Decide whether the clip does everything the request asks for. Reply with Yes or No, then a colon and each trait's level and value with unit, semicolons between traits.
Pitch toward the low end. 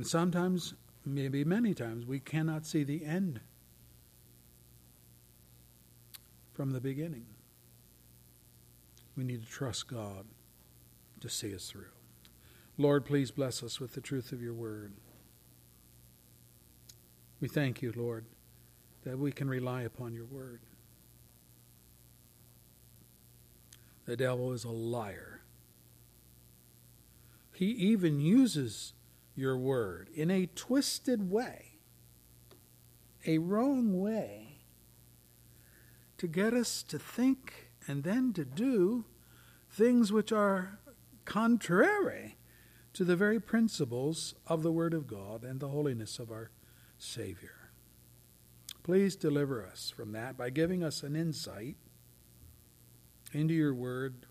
Yes: low, 120 Hz